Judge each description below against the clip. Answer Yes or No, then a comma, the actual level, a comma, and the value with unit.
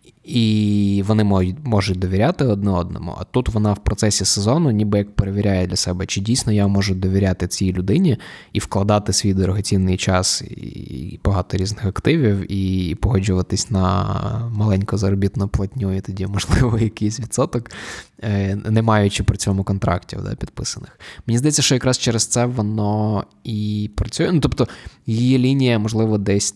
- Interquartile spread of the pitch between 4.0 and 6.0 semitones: No, average, 2.7 semitones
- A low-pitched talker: Yes, low, 100 Hz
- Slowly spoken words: No, average, 150 wpm